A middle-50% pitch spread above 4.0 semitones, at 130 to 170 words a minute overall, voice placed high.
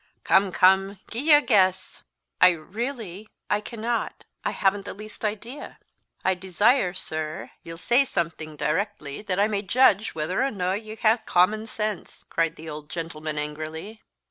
Yes: average, 4.6 semitones; average, 155 wpm; high, 195 Hz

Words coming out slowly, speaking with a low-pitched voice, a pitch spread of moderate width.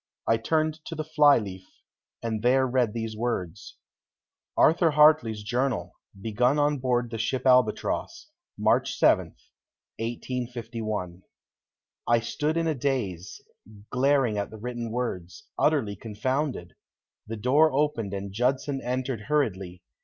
Yes: slow, 125 wpm; low, 125 Hz; average, 4.6 semitones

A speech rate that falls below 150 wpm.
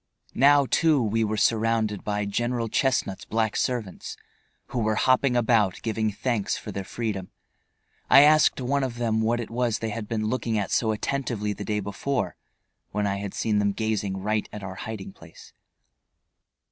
No: average, 170 wpm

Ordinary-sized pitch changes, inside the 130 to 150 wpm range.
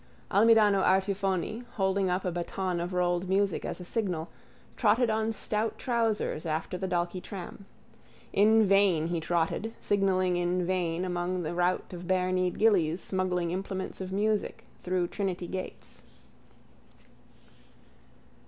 No: narrow, 2.2 semitones; slow, 135 wpm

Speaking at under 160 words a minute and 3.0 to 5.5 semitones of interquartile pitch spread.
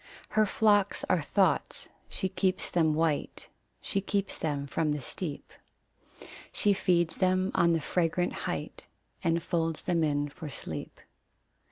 Yes: average, 140 wpm; average, 3.5 semitones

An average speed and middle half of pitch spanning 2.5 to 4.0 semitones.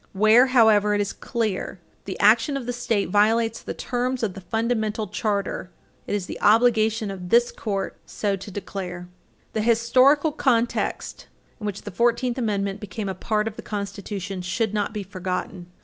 Yes: average, 175 wpm; average, 2.8 semitones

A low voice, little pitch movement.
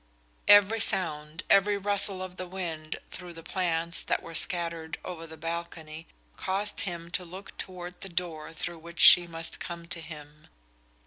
No: medium, 170 Hz; narrow, 2.3 semitones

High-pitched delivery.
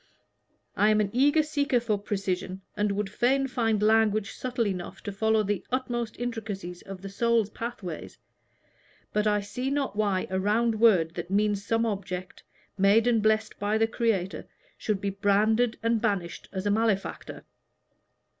Yes: high, 215 Hz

